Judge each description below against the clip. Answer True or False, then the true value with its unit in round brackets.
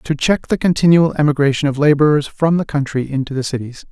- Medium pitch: True (145 Hz)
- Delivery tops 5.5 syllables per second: True (6.0 syllables/s)